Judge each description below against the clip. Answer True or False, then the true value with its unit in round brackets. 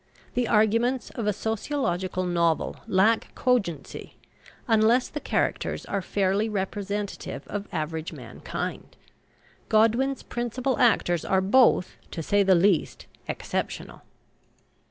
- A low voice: False (205 Hz)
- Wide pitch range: False (3.8 semitones)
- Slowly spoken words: True (110 wpm)